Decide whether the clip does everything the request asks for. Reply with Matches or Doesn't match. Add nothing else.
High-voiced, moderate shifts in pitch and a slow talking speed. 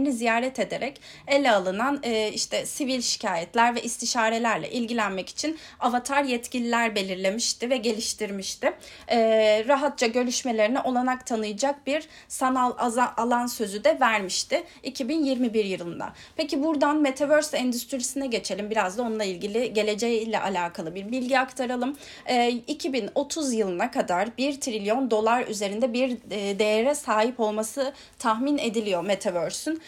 Doesn't match